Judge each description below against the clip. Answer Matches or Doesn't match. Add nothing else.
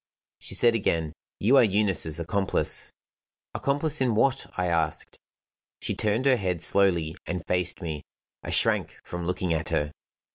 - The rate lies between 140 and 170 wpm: Matches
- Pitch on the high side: Doesn't match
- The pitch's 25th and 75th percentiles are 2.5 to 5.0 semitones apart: Doesn't match